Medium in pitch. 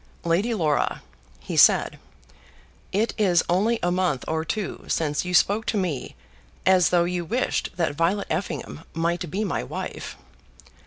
Yes: medium, 175 Hz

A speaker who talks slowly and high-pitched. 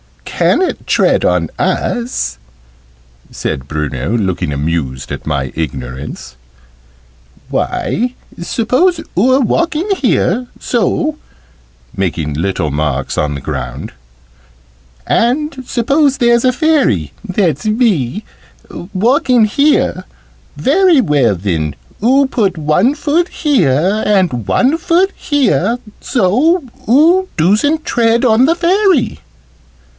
Yes: slow, 105 wpm; high, 220 Hz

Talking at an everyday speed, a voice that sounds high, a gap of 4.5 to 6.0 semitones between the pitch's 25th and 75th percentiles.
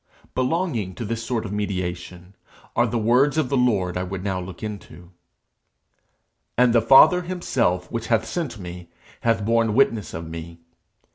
No: average, 160 wpm; low, 110 Hz; average, 5.2 semitones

